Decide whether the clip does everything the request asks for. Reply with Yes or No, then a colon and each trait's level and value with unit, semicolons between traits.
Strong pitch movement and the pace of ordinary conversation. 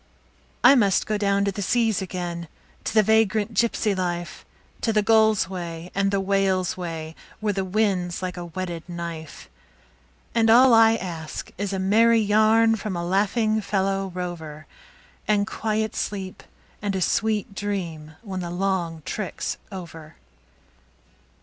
No: average, 3.5 semitones; average, 150 wpm